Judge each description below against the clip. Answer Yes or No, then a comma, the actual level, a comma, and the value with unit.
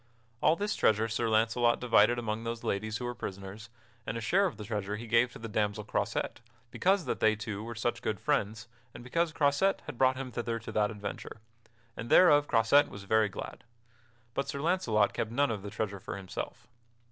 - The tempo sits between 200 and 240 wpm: Yes, fast, 205 wpm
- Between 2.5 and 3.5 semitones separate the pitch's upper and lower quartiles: Yes, average, 3.2 semitones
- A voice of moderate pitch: No, low, 115 Hz